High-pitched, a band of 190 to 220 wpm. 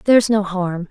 Yes: high, 195 Hz; average, 200 wpm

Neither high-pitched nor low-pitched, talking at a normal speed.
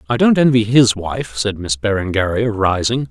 No: low, 110 Hz; average, 175 wpm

